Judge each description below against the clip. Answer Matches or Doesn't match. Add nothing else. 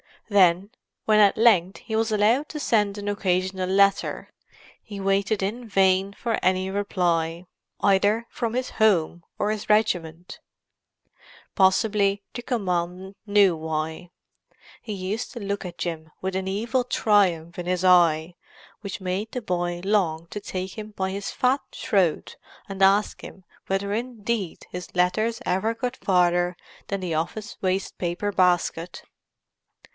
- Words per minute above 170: Doesn't match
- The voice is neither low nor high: Doesn't match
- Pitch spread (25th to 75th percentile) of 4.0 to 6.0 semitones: Doesn't match